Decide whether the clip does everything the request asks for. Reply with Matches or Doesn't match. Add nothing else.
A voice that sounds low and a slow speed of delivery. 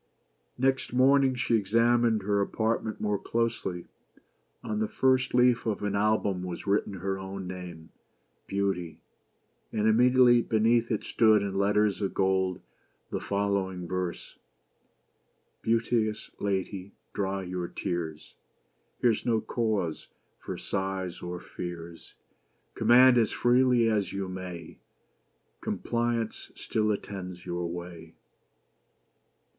Matches